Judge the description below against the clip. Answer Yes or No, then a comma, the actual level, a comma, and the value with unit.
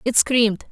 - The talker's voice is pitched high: Yes, high, 230 Hz